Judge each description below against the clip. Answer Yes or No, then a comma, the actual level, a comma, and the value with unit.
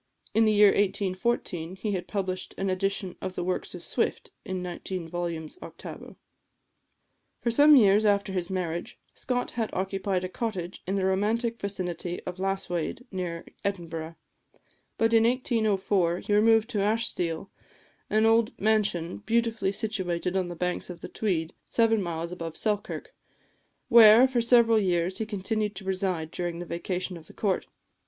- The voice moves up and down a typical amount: Yes, average, 3.6 semitones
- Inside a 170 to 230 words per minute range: No, average, 155 wpm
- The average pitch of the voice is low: No, high, 195 Hz